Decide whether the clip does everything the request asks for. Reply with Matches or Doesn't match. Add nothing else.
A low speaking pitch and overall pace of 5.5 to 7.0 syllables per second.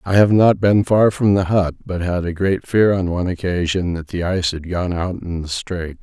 Doesn't match